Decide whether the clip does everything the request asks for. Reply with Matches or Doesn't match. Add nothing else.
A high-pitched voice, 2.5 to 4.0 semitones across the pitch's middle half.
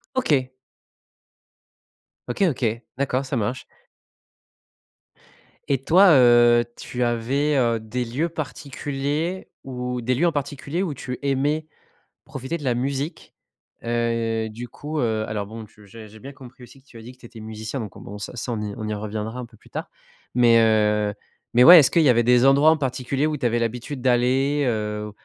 Doesn't match